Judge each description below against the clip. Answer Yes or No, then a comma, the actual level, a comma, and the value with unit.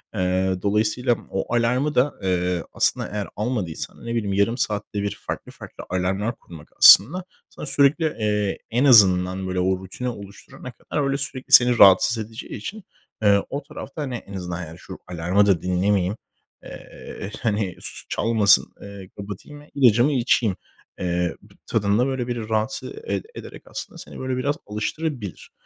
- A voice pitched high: No, low, 105 Hz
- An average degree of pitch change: Yes, average, 4.7 semitones